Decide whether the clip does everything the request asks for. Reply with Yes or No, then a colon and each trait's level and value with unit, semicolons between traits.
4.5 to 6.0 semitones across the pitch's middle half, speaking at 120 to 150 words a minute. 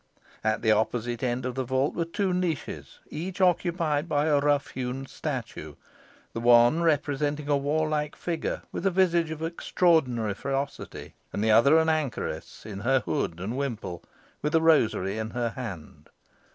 No: average, 5.1 semitones; average, 165 wpm